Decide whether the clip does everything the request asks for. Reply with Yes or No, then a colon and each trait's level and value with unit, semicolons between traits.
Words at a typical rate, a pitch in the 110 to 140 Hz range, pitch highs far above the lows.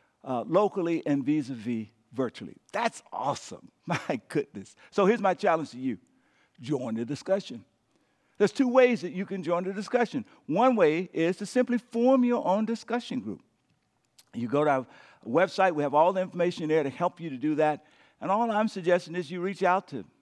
No: average, 195 wpm; medium, 180 Hz; wide, 6.2 semitones